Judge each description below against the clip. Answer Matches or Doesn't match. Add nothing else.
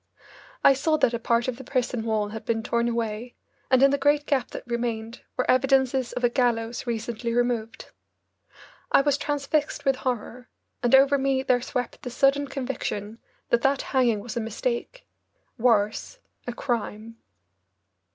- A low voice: Doesn't match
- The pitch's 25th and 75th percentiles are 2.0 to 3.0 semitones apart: Matches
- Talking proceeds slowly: Doesn't match